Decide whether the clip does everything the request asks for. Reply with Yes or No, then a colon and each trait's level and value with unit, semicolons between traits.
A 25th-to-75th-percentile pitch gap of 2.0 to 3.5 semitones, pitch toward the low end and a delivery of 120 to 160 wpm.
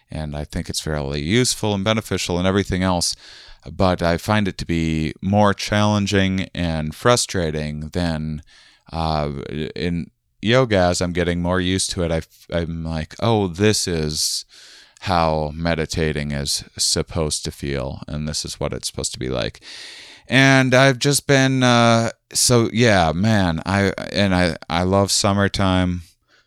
No: average, 4.6 semitones; very low, 90 Hz; average, 150 wpm